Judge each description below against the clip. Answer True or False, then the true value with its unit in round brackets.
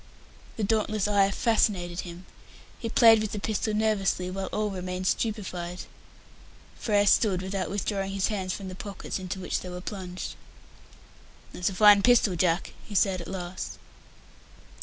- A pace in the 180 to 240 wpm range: False (155 wpm)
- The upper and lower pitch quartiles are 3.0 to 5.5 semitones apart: False (2.4 semitones)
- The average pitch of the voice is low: False (195 Hz)